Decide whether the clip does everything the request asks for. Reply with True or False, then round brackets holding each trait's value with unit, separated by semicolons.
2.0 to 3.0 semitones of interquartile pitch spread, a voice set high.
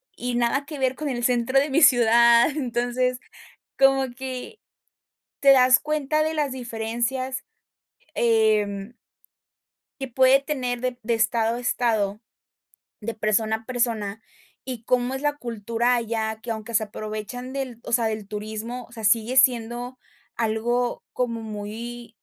True (2.5 semitones; 240 Hz)